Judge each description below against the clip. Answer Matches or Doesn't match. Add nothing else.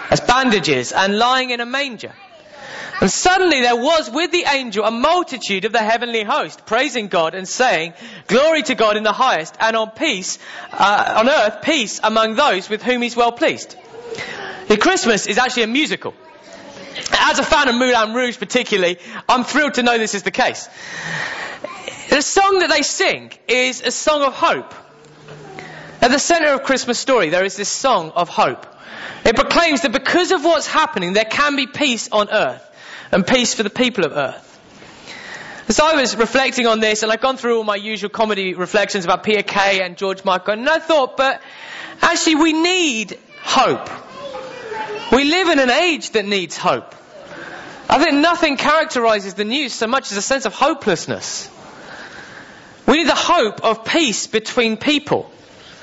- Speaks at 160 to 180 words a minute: Matches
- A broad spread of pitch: Matches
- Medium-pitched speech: Doesn't match